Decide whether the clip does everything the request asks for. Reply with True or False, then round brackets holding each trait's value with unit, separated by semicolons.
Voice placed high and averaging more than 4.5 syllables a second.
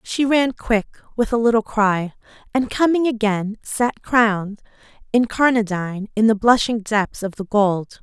False (220 Hz; 4.4 syllables/s)